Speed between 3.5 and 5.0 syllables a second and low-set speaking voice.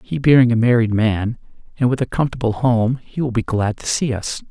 No: 5.3 syllables/s; low, 120 Hz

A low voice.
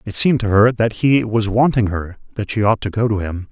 Yes: low, 110 Hz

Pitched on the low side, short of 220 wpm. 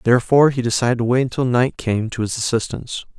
Yes: low, 120 Hz; fast, 205 wpm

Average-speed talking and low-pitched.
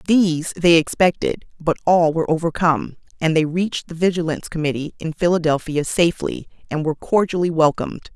No: average, 145 wpm; medium, 165 Hz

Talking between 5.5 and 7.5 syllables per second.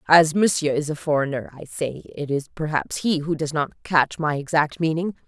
No: 5.0 syllables/s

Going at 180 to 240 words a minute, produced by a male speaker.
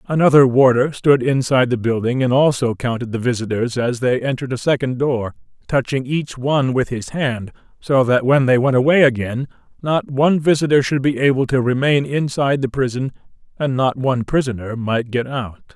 Yes: average, 185 wpm; male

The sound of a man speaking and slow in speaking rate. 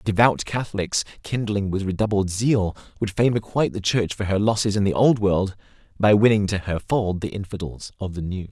No: male; average, 195 wpm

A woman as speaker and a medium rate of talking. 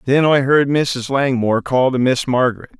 No: male; average, 195 wpm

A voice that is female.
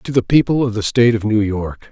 No: male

